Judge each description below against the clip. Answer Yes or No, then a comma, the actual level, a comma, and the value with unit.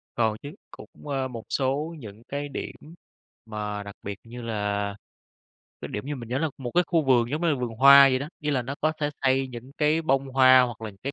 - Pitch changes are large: No, average, 3.8 semitones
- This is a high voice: No, low, 130 Hz